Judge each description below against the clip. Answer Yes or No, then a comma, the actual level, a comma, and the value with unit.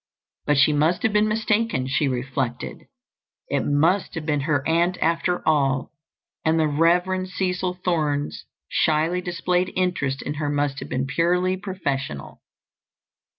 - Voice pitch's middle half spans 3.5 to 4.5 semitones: Yes, average, 4.2 semitones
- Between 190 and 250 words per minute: No, average, 140 wpm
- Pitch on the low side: No, medium, 160 Hz